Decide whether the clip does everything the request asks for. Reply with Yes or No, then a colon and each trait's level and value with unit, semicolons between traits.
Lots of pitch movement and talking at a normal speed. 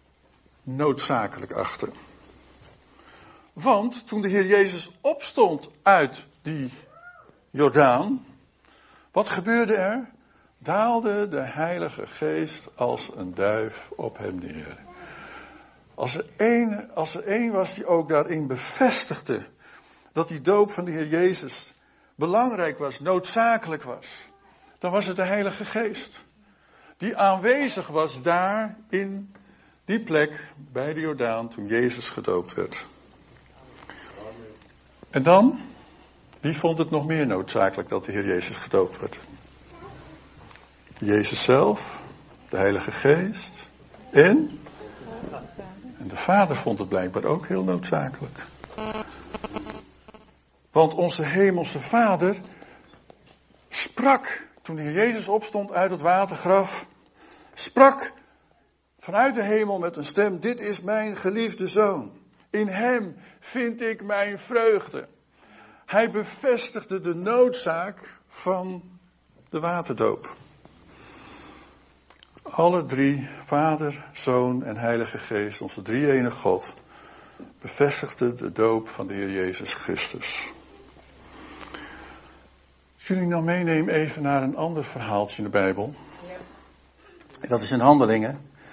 No: wide, 7.4 semitones; slow, 110 wpm